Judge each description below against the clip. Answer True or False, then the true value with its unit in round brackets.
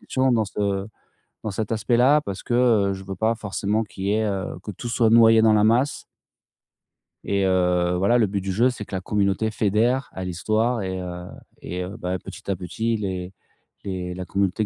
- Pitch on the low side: True (100 Hz)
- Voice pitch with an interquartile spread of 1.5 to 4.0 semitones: True (3.1 semitones)